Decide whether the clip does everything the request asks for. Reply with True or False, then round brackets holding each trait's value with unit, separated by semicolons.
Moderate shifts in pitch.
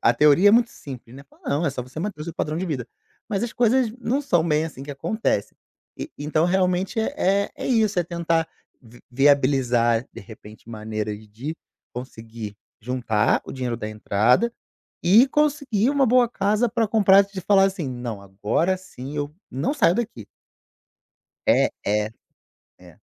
False (9.0 semitones)